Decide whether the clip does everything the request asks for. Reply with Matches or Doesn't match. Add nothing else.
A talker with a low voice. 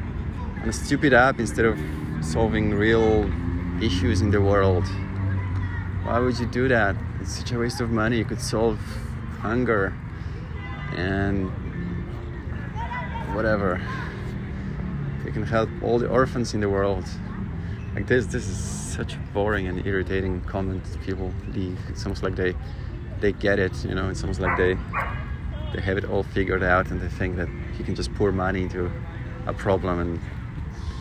Matches